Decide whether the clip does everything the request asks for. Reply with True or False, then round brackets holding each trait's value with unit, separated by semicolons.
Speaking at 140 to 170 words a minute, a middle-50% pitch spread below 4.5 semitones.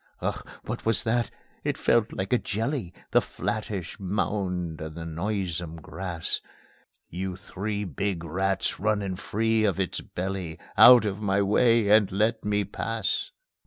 True (145 wpm; 3.1 semitones)